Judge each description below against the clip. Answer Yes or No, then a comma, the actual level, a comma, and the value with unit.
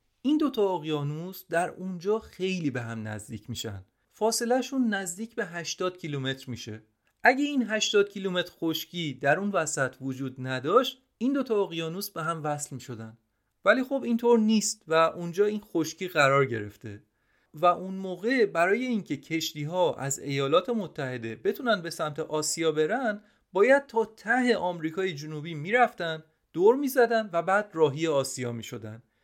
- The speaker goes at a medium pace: Yes, average, 145 wpm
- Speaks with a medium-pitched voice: Yes, medium, 170 Hz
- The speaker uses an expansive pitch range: Yes, wide, 7.6 semitones